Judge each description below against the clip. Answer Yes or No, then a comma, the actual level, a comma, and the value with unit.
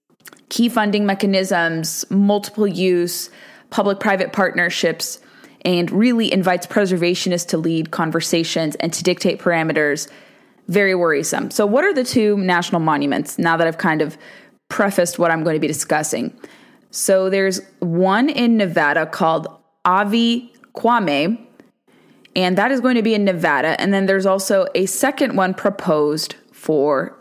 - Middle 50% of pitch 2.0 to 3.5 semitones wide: No, average, 3.9 semitones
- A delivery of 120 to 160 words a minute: Yes, average, 145 wpm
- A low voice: No, high, 190 Hz